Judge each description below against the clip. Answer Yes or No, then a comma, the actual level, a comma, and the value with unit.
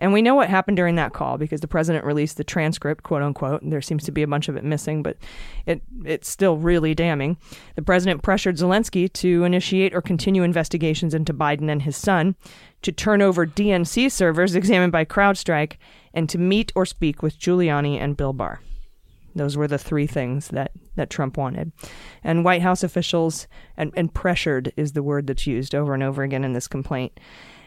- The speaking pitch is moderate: Yes, medium, 165 Hz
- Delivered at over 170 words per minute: Yes, average, 200 wpm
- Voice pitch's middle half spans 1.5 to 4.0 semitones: Yes, average, 3.6 semitones